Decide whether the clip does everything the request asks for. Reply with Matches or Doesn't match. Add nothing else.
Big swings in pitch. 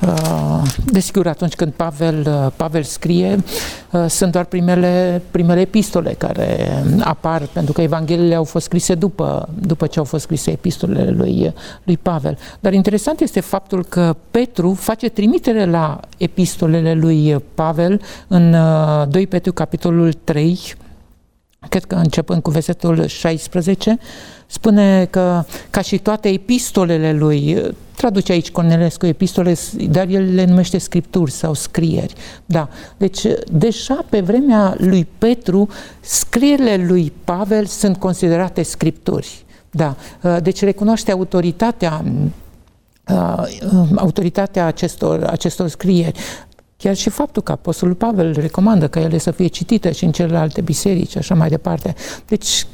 Doesn't match